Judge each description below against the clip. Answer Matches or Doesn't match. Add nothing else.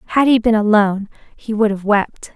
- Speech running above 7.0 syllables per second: Doesn't match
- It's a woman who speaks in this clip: Matches